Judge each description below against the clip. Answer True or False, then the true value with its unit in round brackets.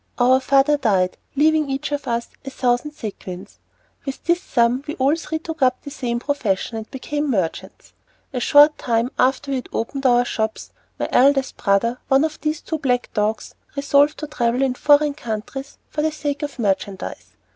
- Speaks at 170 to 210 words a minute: True (175 wpm)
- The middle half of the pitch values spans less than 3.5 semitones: False (3.8 semitones)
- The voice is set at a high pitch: True (270 Hz)